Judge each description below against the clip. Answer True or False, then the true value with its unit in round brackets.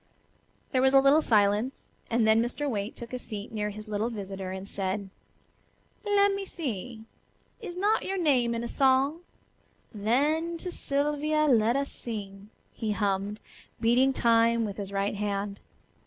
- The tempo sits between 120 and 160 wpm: True (155 wpm)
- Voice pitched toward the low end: False (230 Hz)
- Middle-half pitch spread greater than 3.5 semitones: True (5.4 semitones)